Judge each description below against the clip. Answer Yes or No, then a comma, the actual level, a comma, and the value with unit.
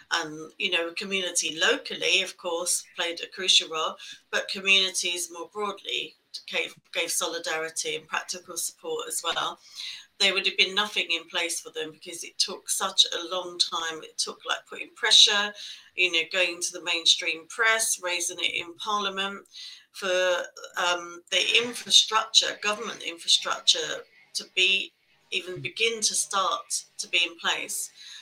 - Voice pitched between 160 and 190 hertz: Yes, medium, 185 Hz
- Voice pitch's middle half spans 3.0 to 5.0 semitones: Yes, average, 3.4 semitones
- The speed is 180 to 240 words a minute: No, average, 150 wpm